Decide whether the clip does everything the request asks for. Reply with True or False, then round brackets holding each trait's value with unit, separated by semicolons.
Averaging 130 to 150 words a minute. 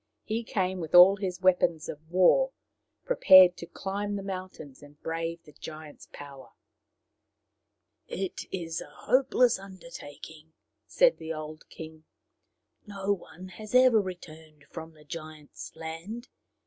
True (135 wpm)